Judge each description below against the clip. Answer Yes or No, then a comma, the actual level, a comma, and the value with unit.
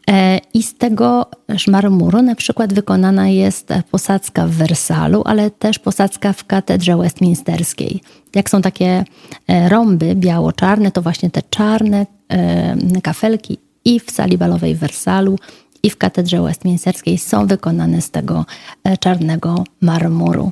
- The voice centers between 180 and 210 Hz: Yes, high, 190 Hz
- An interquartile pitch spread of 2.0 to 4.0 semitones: Yes, average, 3.1 semitones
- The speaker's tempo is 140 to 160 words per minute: No, average, 125 wpm